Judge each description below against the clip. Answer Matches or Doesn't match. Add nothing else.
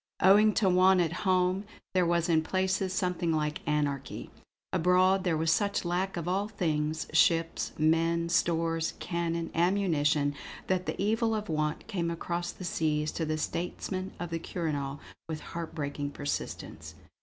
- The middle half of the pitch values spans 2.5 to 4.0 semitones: Matches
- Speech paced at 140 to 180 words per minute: Matches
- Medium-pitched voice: Matches